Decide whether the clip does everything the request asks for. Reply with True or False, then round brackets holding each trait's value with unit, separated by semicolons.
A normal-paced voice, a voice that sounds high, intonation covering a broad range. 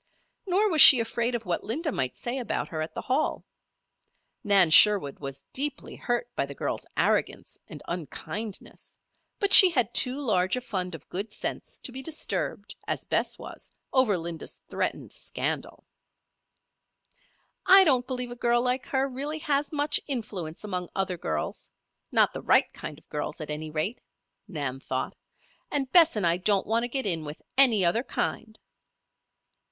True (170 wpm; 225 Hz; 7.3 semitones)